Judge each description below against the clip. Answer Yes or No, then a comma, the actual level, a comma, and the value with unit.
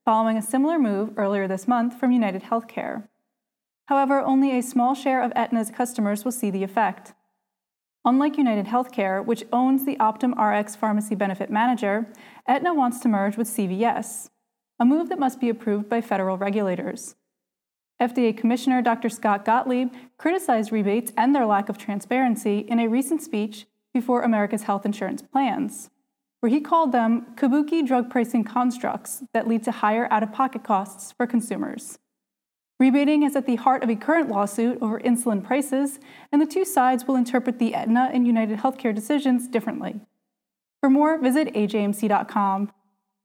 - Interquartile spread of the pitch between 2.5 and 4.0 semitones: Yes, average, 3.3 semitones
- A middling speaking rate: Yes, average, 160 wpm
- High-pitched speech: Yes, high, 235 Hz